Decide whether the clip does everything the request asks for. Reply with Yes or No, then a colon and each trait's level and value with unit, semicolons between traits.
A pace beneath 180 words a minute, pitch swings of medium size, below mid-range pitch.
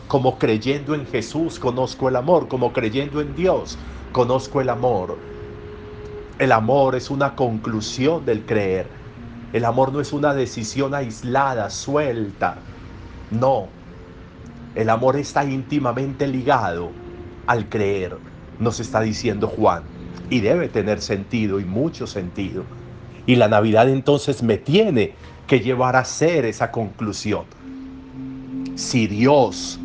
Yes: slow, 125 wpm; average, 4.5 semitones; low, 115 Hz